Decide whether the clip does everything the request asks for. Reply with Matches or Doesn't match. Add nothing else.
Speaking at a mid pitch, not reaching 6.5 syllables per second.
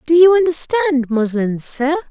Doesn't match